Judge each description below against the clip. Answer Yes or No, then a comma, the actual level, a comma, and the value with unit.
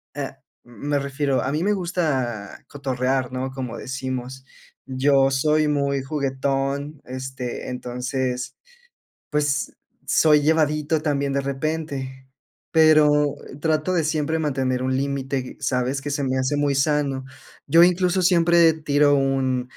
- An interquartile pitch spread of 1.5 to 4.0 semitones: Yes, narrow, 2.5 semitones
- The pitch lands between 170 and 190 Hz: No, medium, 140 Hz